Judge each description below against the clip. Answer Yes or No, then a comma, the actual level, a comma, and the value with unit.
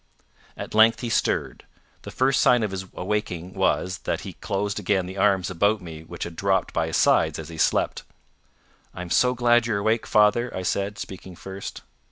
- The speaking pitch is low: Yes, low, 100 Hz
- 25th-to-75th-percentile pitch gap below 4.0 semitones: Yes, average, 3.2 semitones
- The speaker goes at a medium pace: Yes, average, 190 wpm